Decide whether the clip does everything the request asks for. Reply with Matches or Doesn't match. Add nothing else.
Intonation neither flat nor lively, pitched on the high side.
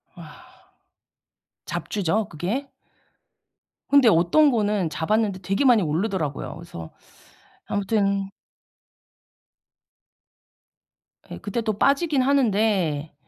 Matches